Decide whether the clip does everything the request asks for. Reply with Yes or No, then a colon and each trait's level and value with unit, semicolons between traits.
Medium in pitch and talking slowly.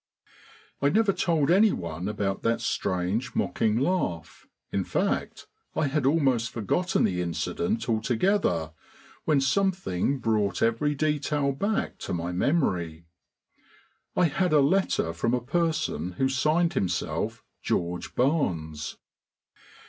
No: low, 130 Hz; slow, 120 wpm